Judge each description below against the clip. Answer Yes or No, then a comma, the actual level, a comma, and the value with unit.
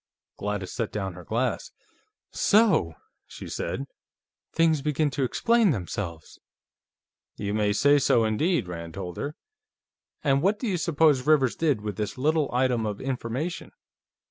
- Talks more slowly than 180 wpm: Yes, average, 145 wpm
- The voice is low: Yes, low, 130 Hz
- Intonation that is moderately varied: No, wide, 6.9 semitones